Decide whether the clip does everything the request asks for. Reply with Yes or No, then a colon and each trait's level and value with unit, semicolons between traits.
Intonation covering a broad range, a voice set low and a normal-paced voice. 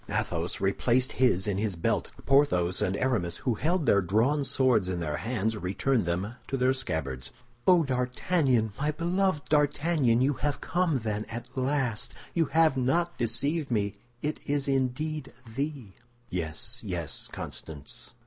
Yes: wide, 6.3 semitones; low, 125 Hz; average, 150 wpm